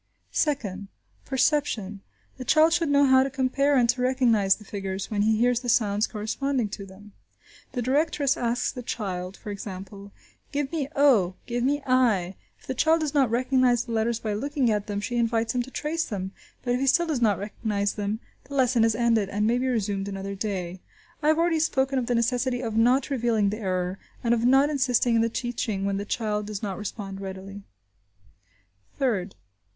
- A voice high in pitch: Yes, high, 235 Hz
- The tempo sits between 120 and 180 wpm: No, average, 195 wpm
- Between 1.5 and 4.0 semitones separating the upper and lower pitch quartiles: No, average, 4.4 semitones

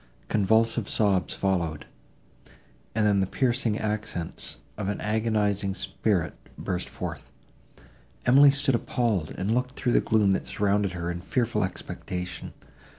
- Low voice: Yes, low, 105 Hz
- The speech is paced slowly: Yes, slow, 130 wpm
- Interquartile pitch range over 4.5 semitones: No, average, 3.3 semitones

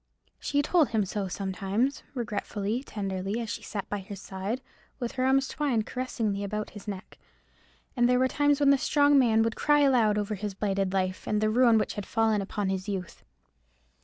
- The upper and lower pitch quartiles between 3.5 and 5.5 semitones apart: Yes, average, 4.4 semitones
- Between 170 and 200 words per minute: Yes, average, 190 wpm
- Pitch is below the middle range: No, high, 215 Hz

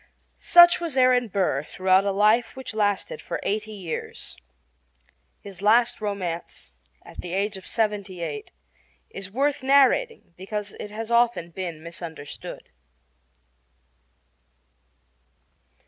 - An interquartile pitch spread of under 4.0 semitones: No, average, 4.7 semitones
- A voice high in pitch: Yes, high, 210 Hz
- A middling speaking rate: No, slow, 115 wpm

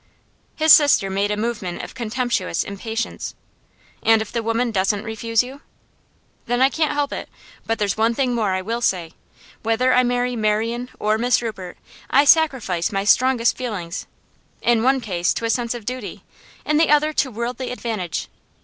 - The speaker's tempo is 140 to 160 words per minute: No, average, 175 wpm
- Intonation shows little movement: No, average, 3.2 semitones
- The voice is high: Yes, high, 230 Hz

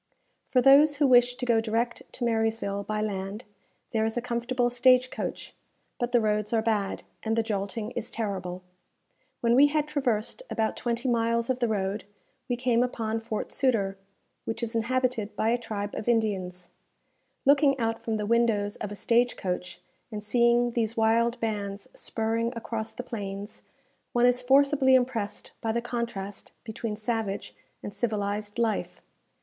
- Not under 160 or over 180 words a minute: Yes, average, 165 wpm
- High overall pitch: Yes, high, 225 Hz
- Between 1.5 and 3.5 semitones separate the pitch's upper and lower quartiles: Yes, narrow, 2.5 semitones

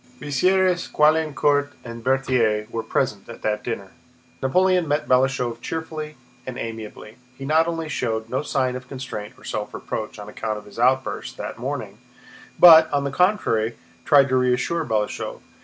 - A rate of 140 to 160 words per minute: Yes, average, 155 wpm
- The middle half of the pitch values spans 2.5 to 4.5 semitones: No, average, 5.1 semitones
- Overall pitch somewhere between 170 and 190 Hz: No, low, 130 Hz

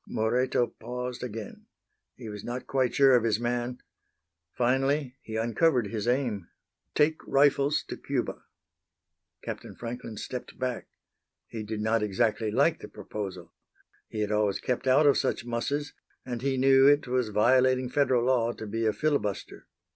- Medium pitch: No, low, 125 Hz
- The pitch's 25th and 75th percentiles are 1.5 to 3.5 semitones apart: Yes, average, 3.1 semitones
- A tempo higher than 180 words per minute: No, average, 155 wpm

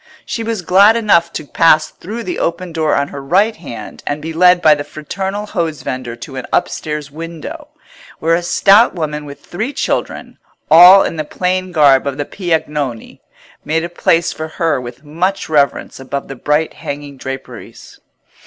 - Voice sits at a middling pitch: Yes, medium, 160 Hz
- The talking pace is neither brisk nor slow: Yes, average, 170 wpm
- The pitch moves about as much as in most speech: Yes, average, 4.0 semitones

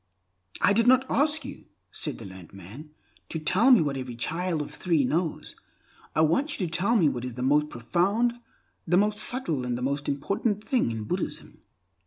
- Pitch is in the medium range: Yes, medium, 160 Hz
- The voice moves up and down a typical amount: No, wide, 8.5 semitones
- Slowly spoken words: No, average, 195 wpm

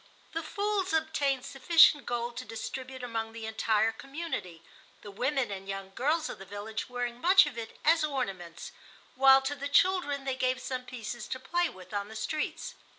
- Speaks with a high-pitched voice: Yes, very high, 255 Hz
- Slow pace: No, average, 180 wpm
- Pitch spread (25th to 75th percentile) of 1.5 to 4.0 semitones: No, average, 4.9 semitones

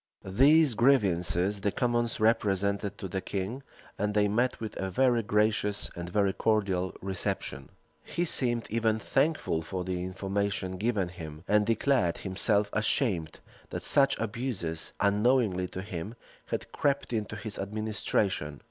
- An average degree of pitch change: Yes, average, 3.6 semitones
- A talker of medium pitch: No, low, 105 Hz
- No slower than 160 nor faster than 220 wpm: No, average, 140 wpm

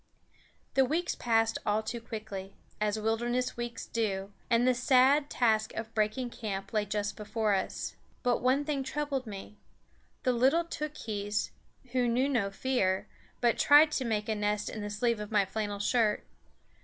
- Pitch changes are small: No, average, 3.3 semitones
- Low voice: No, high, 225 Hz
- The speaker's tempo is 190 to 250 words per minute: No, average, 165 wpm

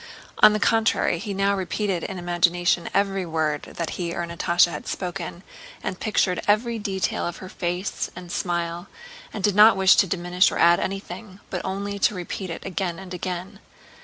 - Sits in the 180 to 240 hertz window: Yes, medium, 185 Hz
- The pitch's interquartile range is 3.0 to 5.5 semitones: No, narrow, 2.4 semitones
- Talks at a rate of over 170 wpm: Yes, average, 180 wpm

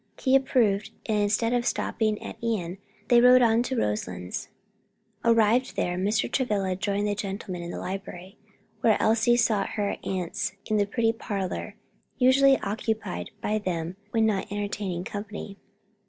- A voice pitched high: Yes, high, 210 Hz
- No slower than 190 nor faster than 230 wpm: No, average, 150 wpm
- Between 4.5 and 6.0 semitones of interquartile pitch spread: No, average, 2.9 semitones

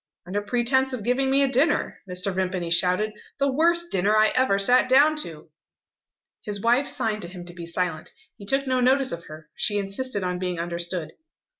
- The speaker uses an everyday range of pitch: No, wide, 6.4 semitones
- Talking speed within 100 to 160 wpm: No, average, 190 wpm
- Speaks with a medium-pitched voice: No, high, 205 Hz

